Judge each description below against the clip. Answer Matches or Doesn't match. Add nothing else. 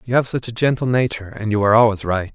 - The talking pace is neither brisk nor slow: Doesn't match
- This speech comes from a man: Matches